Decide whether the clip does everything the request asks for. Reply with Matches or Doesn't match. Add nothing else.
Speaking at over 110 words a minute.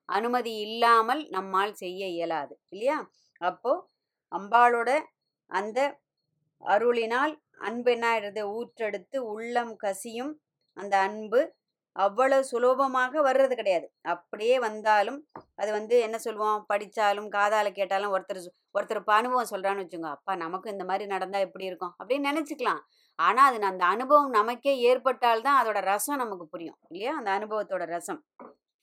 Matches